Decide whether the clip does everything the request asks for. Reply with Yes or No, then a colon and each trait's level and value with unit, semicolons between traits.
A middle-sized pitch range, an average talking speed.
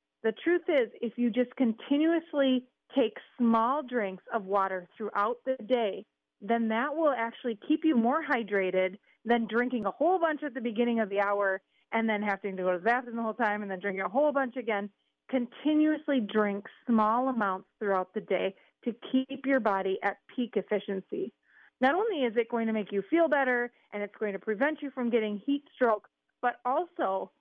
Yes: average, 4.3 semitones; average, 195 wpm